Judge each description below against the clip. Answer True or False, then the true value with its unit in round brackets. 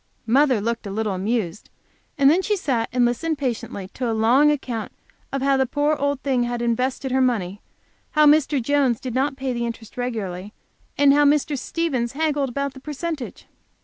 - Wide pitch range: False (3.5 semitones)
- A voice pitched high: True (260 Hz)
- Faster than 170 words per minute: True (185 wpm)